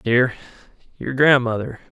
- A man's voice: Yes, male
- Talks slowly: Yes, slow, 90 wpm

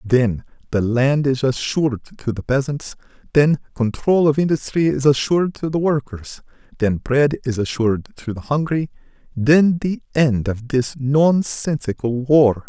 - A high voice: No, low, 135 Hz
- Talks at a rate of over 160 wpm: No, average, 145 wpm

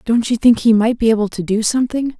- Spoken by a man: No, female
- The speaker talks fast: Yes, fast, 275 wpm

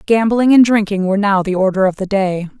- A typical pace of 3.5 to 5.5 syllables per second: No, 5.8 syllables/s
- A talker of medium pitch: No, high, 200 Hz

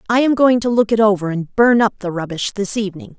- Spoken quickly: Yes, fast, 265 wpm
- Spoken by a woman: Yes, female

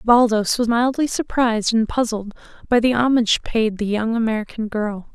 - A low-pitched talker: No, high, 225 Hz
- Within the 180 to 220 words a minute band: No, average, 165 wpm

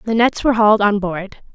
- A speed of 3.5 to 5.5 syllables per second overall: No, 6.8 syllables/s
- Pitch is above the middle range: Yes, high, 210 Hz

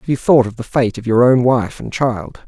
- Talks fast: Yes, fast, 290 wpm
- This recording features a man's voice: Yes, male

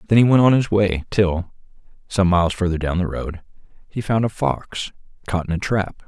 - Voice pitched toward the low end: Yes, very low, 95 Hz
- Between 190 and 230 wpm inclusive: Yes, fast, 205 wpm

